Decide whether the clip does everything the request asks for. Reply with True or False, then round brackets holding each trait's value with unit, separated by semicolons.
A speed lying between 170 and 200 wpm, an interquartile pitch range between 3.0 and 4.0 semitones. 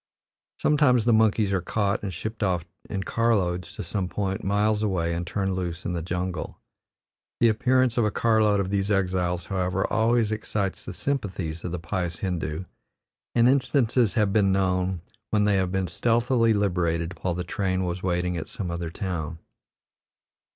True (175 wpm; 3.5 semitones)